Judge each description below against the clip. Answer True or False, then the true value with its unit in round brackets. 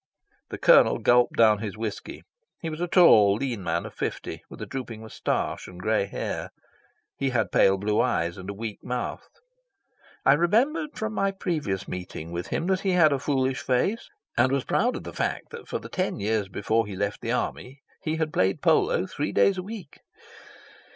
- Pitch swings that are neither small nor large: False (7.9 semitones)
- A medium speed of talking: True (195 wpm)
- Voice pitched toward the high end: False (125 Hz)